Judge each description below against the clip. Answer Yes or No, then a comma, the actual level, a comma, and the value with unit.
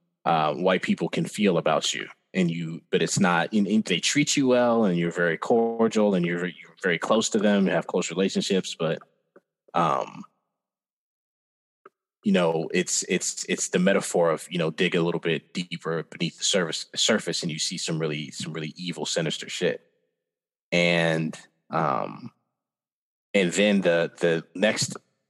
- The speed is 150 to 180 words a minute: Yes, average, 170 wpm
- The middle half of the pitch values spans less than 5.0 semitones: No, wide, 5.4 semitones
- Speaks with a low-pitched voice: Yes, very low, 85 Hz